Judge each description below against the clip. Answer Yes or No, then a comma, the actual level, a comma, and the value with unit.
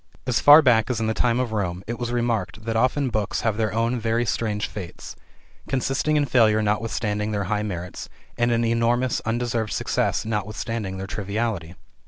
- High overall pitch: No, low, 115 Hz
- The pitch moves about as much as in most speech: No, narrow, 2.2 semitones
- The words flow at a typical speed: Yes, average, 180 wpm